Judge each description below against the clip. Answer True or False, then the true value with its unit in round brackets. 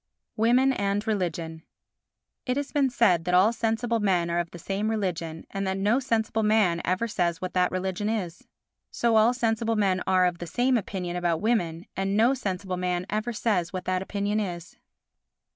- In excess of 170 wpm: True (185 wpm)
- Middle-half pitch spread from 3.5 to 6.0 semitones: True (3.8 semitones)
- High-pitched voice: True (195 Hz)